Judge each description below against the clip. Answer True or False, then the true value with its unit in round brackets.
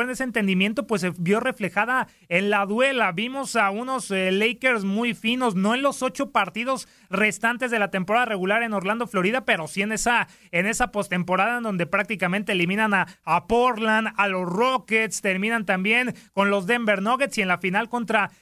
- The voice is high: True (215 Hz)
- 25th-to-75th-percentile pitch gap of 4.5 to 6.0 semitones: False (3.5 semitones)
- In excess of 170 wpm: True (190 wpm)